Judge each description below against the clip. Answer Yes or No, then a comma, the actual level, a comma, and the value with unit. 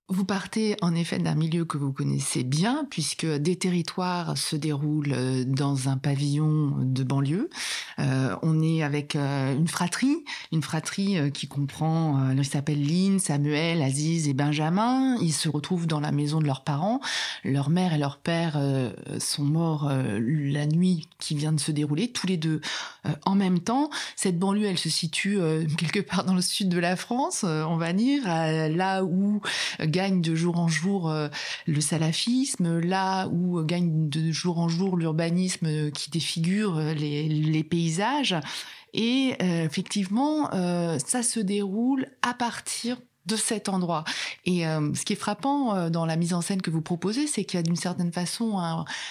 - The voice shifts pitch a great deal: No, average, 4.0 semitones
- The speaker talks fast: No, average, 165 wpm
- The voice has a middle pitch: Yes, medium, 170 Hz